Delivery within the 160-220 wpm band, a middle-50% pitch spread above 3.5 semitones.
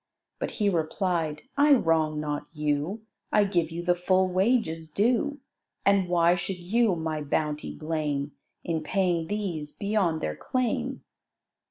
No: average, 140 wpm; average, 4.2 semitones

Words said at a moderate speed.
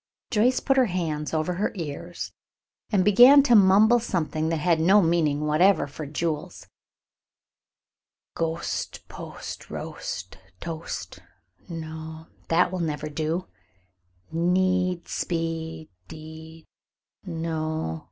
No: slow, 105 wpm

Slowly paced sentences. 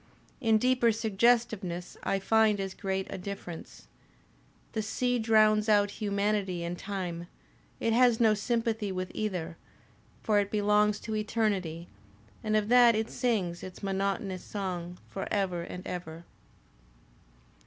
Yes: slow, 130 wpm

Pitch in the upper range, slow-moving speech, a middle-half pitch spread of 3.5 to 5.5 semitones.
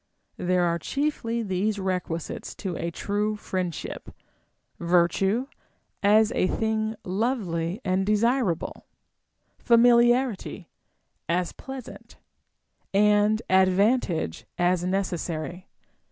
Yes: high, 195 Hz; slow, 90 wpm; average, 3.8 semitones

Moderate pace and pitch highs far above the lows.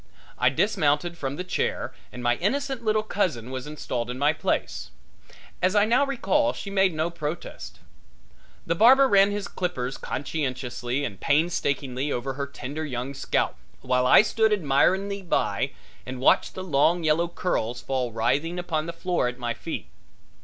Yes: average, 160 wpm; wide, 6.6 semitones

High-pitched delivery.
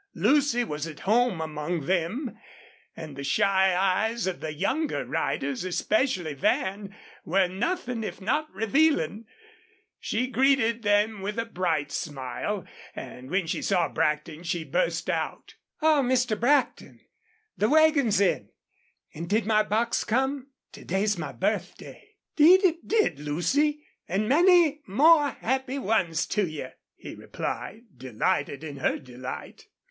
Yes: high, 210 Hz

